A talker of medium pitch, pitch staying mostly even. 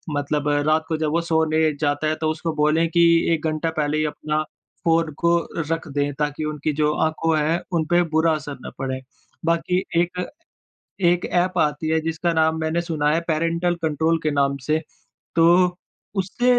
Yes: medium, 160 Hz; narrow, 1.6 semitones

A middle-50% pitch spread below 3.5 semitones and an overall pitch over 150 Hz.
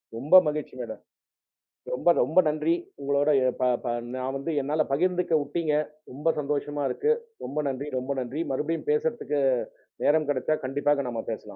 No: average, 2.9 semitones; medium, 145 Hz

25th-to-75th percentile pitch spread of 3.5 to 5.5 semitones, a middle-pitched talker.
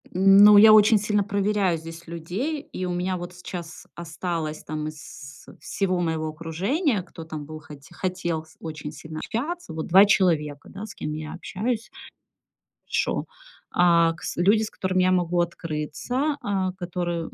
Yes: average, 3.8 semitones; medium, 175 Hz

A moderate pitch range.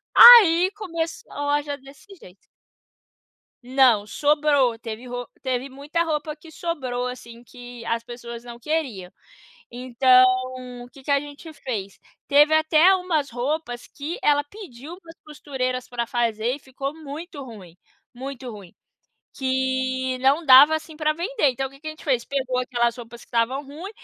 Yes: average, 3.9 semitones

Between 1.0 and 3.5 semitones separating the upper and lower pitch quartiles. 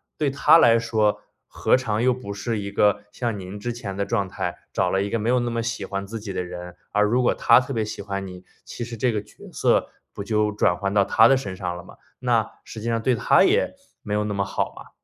Yes: average, 3.0 semitones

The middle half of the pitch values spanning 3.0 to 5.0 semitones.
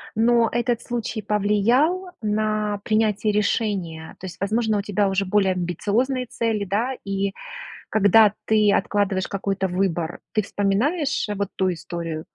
No: narrow, 2.5 semitones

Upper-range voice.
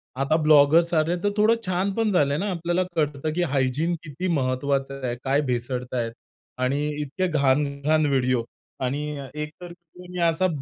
No: medium, 150 Hz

